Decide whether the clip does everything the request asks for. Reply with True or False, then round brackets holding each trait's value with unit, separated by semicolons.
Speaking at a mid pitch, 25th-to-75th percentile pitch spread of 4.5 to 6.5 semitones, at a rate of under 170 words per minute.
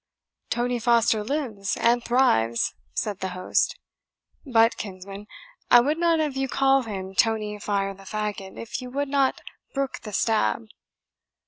False (225 Hz; 5.0 semitones; 145 wpm)